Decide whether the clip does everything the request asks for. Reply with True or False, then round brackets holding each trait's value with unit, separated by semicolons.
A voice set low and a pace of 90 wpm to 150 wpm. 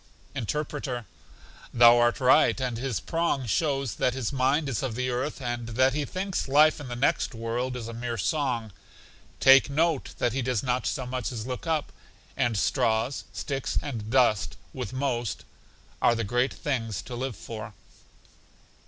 False (125 Hz; 170 wpm)